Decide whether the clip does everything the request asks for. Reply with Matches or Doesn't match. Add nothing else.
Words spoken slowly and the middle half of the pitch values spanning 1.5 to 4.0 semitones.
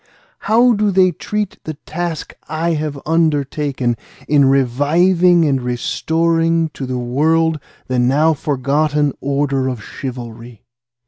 Matches